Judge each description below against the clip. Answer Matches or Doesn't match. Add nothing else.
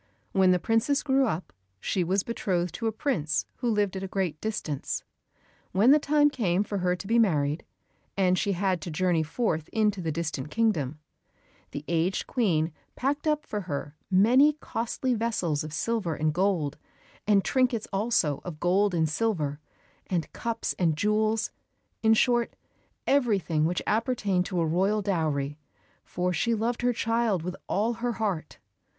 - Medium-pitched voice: Doesn't match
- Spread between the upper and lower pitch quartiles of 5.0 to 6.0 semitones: Matches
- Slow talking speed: Doesn't match